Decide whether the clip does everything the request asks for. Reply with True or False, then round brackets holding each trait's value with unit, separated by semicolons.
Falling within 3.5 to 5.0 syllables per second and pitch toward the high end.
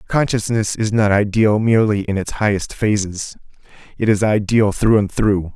False (4.8 syllables/s; 105 Hz)